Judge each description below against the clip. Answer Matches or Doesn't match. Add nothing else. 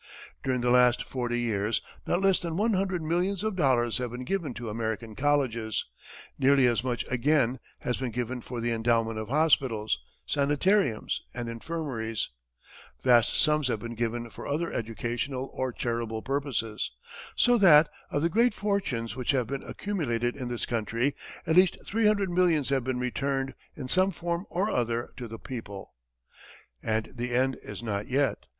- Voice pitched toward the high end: Doesn't match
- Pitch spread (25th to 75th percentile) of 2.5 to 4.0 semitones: Doesn't match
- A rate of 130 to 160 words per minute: Doesn't match